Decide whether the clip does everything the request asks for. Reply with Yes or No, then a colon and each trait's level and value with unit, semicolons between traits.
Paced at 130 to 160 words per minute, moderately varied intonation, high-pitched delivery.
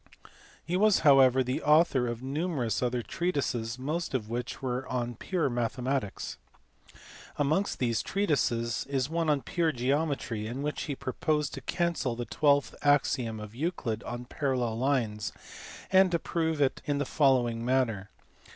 No: average, 150 wpm; average, 4.1 semitones; low, 130 Hz